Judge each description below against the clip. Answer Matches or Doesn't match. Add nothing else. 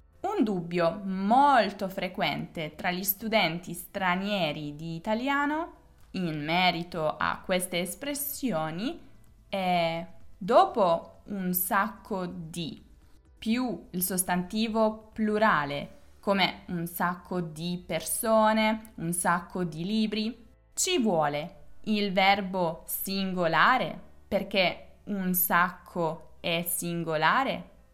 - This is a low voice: Doesn't match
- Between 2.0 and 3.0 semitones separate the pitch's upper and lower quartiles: Doesn't match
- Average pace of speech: Doesn't match